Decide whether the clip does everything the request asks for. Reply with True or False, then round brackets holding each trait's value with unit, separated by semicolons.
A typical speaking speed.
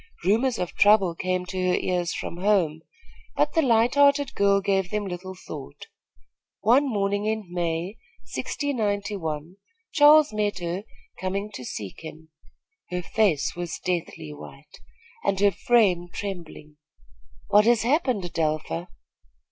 False (130 wpm)